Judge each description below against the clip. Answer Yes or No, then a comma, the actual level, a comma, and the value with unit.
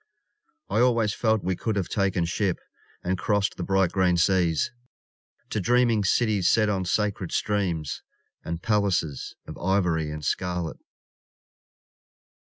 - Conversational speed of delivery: No, slow, 130 wpm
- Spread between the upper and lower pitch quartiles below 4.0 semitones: Yes, average, 3.3 semitones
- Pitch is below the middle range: Yes, very low, 95 Hz